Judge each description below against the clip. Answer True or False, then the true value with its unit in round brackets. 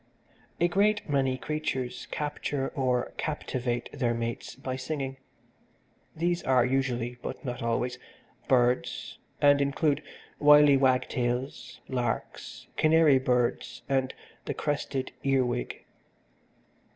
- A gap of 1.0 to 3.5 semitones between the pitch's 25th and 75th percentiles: True (2.9 semitones)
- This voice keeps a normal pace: False (105 wpm)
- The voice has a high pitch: False (130 Hz)